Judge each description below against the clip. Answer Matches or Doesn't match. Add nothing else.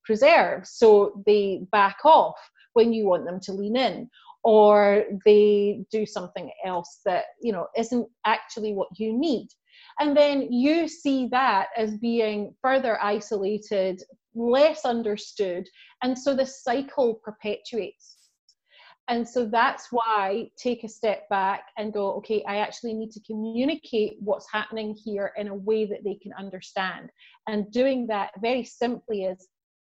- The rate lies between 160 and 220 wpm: Doesn't match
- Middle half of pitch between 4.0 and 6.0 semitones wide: Doesn't match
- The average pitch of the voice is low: Doesn't match